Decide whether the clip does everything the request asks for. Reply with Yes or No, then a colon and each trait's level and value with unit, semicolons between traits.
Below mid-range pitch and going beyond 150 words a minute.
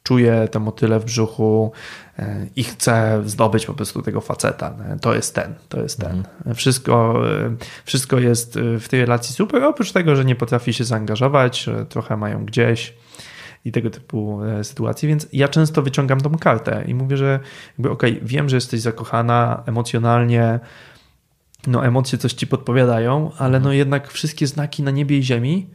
Yes: low, 120 Hz; fast, 160 wpm